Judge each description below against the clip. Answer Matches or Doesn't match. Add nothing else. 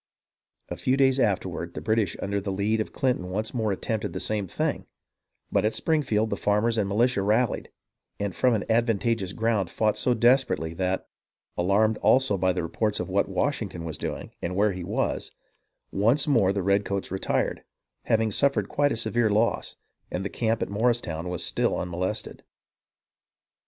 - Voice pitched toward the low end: Matches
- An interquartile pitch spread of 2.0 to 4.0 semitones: Matches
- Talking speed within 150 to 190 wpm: Matches